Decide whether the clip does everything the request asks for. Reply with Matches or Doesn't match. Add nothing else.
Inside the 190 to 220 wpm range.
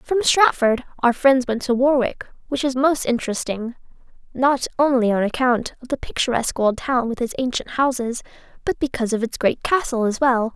Doesn't match